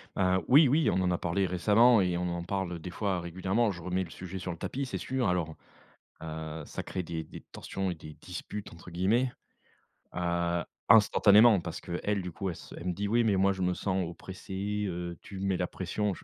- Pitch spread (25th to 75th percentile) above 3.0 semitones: No, average, 2.7 semitones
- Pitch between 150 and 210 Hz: No, very low, 95 Hz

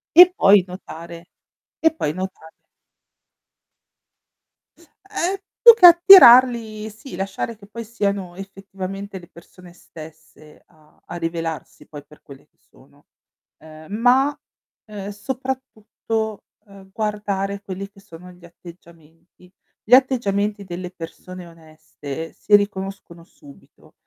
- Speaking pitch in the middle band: No, high, 195 Hz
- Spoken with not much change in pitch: No, average, 4.4 semitones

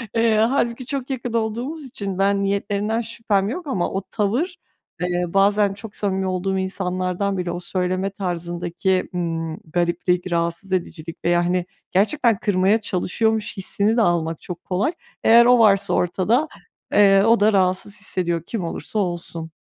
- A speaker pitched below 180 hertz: No, high, 195 Hz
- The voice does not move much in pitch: No, average, 3.6 semitones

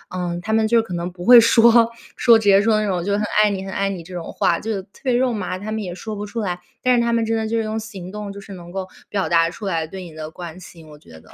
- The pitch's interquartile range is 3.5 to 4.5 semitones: Yes, average, 3.9 semitones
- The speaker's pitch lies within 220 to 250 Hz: No, high, 200 Hz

